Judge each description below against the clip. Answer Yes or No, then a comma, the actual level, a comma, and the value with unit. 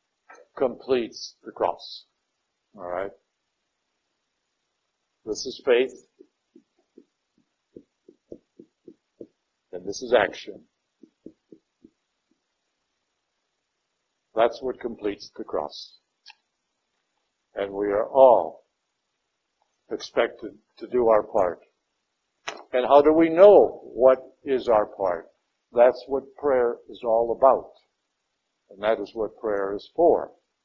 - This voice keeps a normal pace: No, slow, 90 wpm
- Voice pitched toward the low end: Yes, low, 130 Hz